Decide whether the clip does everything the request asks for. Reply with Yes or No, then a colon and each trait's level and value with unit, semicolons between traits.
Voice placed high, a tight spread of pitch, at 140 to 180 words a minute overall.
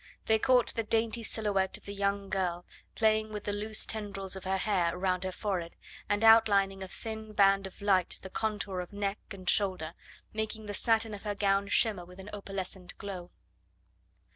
No: high, 200 Hz; narrow, 2.3 semitones; average, 190 wpm